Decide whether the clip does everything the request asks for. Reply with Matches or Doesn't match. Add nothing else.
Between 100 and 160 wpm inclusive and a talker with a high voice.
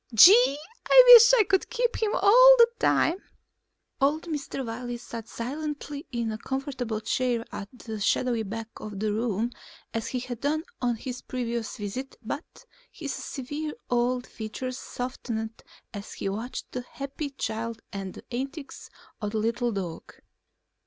Matches